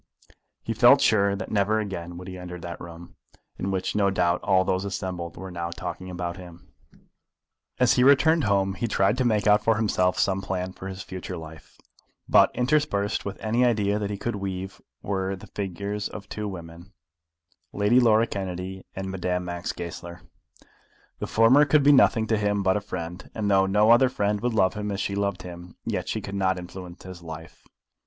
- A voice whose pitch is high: No, very low, 95 Hz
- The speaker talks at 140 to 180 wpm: No, average, 195 wpm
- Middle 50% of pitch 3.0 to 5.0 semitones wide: No, narrow, 2.5 semitones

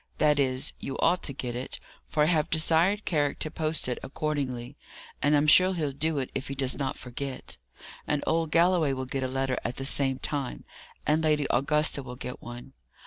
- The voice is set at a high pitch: No, medium, 140 Hz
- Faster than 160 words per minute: Yes, average, 200 wpm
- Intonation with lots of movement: No, average, 2.9 semitones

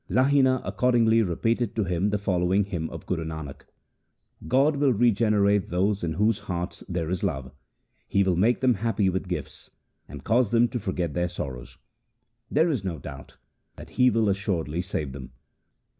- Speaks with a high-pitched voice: No, low, 100 Hz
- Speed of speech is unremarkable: Yes, average, 175 wpm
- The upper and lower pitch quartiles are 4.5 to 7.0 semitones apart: Yes, average, 5.0 semitones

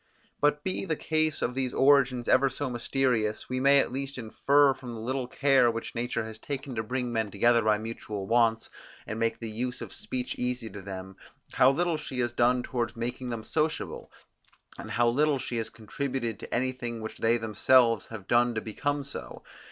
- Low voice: Yes, low, 120 Hz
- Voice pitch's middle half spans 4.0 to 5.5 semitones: No, average, 3.0 semitones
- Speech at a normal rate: Yes, average, 195 wpm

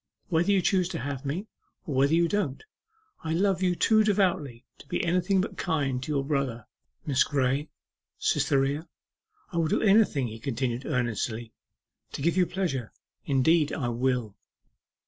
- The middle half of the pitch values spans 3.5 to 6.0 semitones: Yes, wide, 5.5 semitones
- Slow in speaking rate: No, average, 160 wpm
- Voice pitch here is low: No, medium, 145 Hz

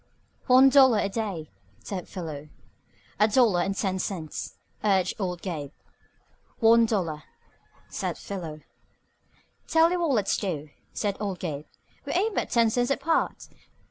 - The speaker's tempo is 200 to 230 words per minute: No, slow, 135 wpm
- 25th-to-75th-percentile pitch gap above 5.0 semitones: Yes, wide, 5.5 semitones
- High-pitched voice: Yes, high, 200 Hz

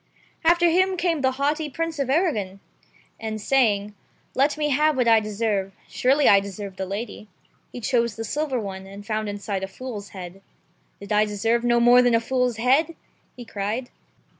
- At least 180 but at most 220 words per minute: Yes, average, 185 wpm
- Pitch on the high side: Yes, high, 235 Hz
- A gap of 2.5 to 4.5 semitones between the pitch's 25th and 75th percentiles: No, average, 5.1 semitones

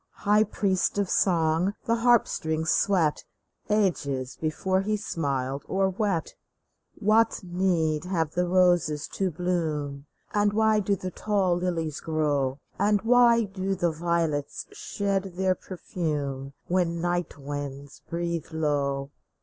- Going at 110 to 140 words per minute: Yes, slow, 135 wpm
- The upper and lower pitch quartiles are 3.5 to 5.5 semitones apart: Yes, average, 4.2 semitones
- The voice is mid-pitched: Yes, medium, 175 Hz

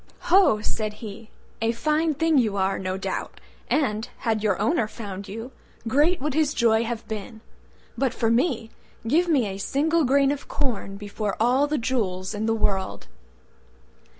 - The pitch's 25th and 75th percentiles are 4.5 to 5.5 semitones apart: Yes, average, 5.1 semitones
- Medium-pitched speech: No, high, 230 Hz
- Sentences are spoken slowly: No, average, 165 wpm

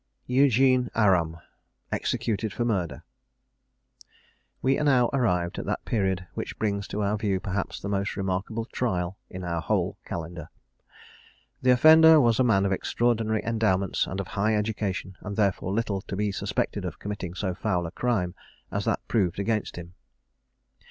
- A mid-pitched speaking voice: No, low, 100 Hz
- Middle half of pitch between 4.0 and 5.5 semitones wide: No, average, 3.6 semitones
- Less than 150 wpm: No, average, 160 wpm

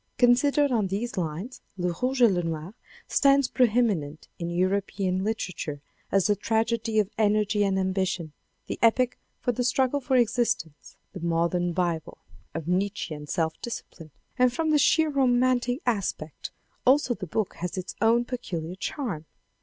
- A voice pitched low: No, high, 205 Hz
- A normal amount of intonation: No, wide, 5.7 semitones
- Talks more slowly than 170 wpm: Yes, average, 155 wpm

